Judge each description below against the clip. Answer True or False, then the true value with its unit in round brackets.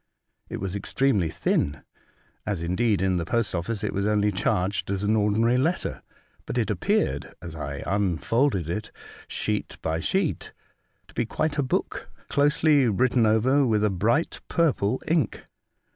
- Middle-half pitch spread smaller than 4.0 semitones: False (5.4 semitones)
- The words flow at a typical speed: True (155 wpm)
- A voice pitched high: False (105 Hz)